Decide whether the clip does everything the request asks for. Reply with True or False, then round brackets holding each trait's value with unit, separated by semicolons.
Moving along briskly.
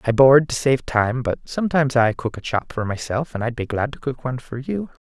True (260 wpm)